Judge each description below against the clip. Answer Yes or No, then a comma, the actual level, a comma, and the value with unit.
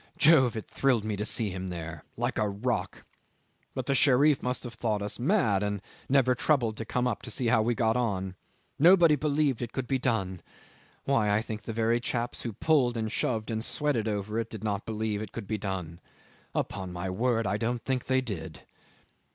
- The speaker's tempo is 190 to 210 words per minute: Yes, average, 200 wpm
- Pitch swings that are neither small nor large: Yes, average, 3.6 semitones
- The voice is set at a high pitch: No, low, 115 Hz